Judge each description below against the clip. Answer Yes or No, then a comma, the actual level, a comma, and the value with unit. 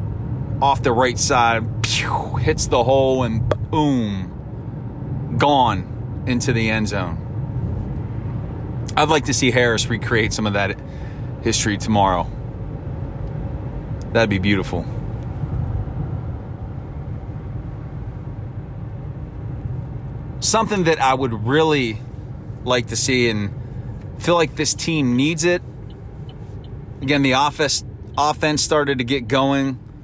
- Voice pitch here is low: Yes, low, 125 Hz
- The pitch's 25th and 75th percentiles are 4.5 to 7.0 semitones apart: No, average, 3.0 semitones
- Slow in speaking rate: Yes, slow, 105 wpm